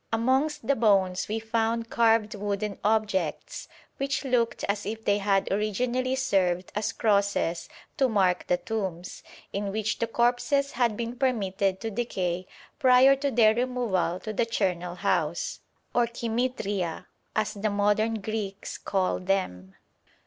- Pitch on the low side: No, high, 215 Hz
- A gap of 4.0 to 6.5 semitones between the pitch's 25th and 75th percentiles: No, average, 3.4 semitones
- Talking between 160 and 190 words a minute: No, average, 140 wpm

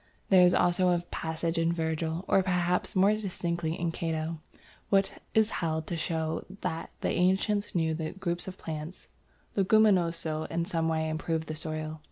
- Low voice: No, medium, 170 Hz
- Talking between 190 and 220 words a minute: No, average, 170 wpm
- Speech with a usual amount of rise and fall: No, narrow, 2.3 semitones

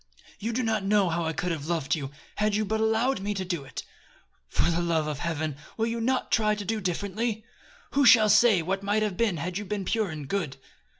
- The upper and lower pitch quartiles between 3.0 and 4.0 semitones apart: No, average, 4.6 semitones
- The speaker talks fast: Yes, fast, 235 wpm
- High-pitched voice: Yes, high, 200 Hz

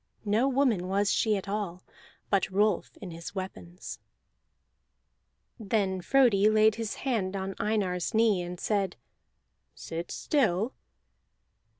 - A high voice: Yes, high, 200 Hz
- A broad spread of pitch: No, average, 2.8 semitones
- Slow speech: Yes, slow, 115 wpm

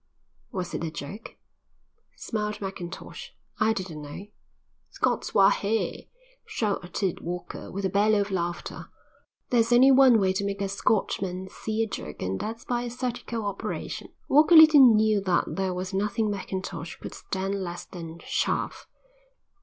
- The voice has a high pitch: Yes, high, 200 Hz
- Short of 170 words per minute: Yes, average, 150 wpm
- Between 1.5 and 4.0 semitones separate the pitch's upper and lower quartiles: Yes, average, 3.3 semitones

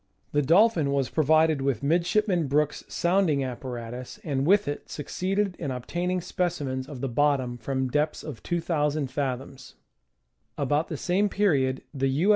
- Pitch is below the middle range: No, medium, 145 Hz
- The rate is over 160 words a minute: No, average, 145 wpm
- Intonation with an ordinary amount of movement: Yes, average, 4.5 semitones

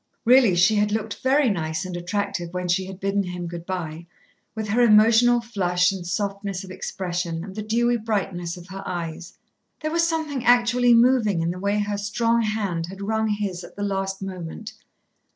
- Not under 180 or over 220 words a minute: Yes, average, 190 wpm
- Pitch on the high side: Yes, high, 200 Hz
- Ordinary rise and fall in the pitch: Yes, average, 3.8 semitones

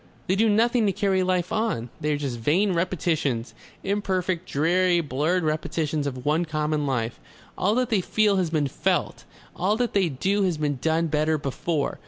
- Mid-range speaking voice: Yes, medium, 170 Hz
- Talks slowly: No, average, 180 wpm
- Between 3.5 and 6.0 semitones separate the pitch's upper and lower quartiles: Yes, average, 4.4 semitones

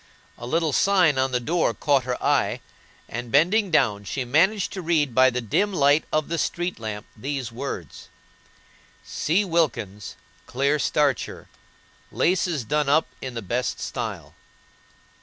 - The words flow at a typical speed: Yes, average, 145 wpm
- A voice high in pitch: No, medium, 140 Hz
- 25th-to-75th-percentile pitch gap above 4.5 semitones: Yes, wide, 5.4 semitones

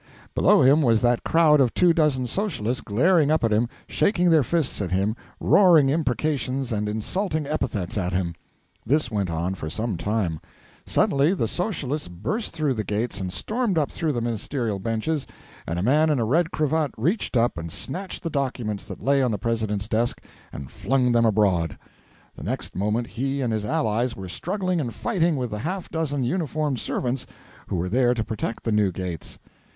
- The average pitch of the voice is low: Yes, low, 125 Hz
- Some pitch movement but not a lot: No, wide, 6.5 semitones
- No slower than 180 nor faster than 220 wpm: Yes, average, 190 wpm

